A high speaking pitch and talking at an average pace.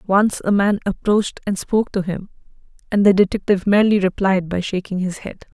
Yes: high, 195 Hz; average, 180 wpm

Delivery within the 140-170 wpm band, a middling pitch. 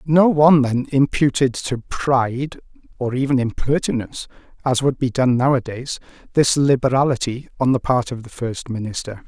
No: average, 150 wpm; low, 130 Hz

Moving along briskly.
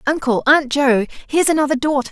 No: average, 170 wpm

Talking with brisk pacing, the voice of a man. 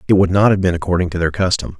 Yes: fast, 300 wpm; male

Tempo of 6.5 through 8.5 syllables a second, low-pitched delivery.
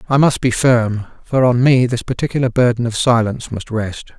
No: 5.3 syllables/s; low, 120 Hz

